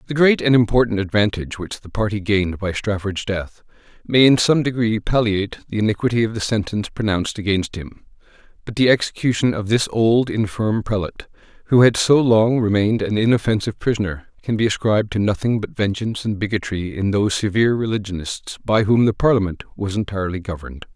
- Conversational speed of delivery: Yes, average, 175 wpm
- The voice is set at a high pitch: No, low, 105 Hz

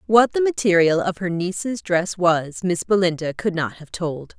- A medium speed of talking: Yes, average, 190 wpm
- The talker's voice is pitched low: No, medium, 185 Hz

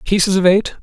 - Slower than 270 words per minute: Yes, fast, 220 wpm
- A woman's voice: No, male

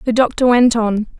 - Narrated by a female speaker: Yes, female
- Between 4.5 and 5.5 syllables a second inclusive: Yes, 5.1 syllables/s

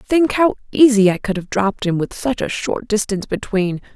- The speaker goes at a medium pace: No, fast, 210 wpm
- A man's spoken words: No, female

